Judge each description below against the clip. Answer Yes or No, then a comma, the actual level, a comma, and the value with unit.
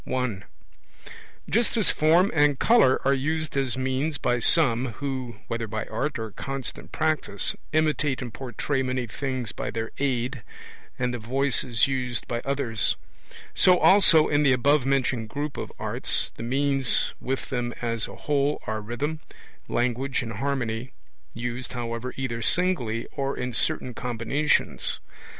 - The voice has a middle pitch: No, low, 130 Hz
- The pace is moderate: Yes, average, 150 wpm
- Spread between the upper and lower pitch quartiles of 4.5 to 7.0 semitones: No, average, 3.2 semitones